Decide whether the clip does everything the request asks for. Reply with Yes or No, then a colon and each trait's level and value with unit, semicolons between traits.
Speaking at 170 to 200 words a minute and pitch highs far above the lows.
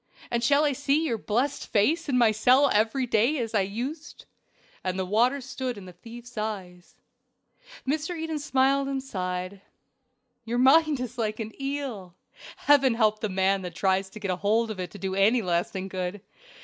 Yes: average, 185 wpm; wide, 5.7 semitones